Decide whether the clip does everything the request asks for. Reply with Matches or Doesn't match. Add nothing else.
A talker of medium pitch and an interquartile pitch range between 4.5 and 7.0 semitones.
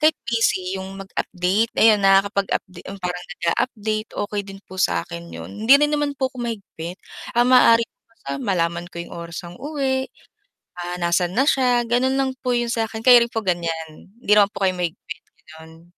Doesn't match